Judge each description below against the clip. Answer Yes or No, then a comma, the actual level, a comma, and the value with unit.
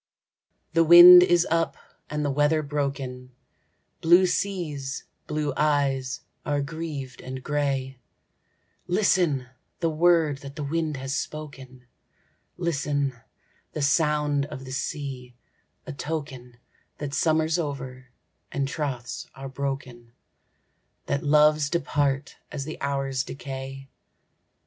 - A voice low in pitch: No, medium, 145 Hz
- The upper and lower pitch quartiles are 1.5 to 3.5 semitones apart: Yes, narrow, 2.5 semitones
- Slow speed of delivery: Yes, slow, 110 wpm